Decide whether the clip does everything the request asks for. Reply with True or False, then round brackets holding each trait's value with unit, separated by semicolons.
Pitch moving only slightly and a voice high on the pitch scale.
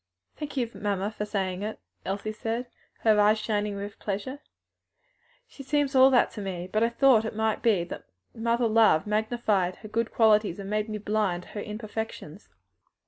True (2.2 semitones; 215 Hz)